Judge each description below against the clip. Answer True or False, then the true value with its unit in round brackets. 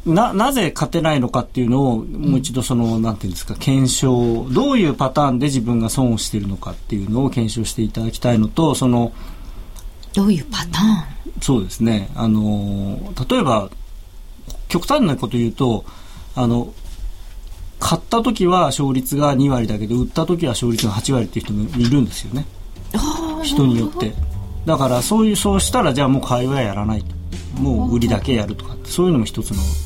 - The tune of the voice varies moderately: True (5.0 semitones)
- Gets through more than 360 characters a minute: True (370 characters per minute)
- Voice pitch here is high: False (120 Hz)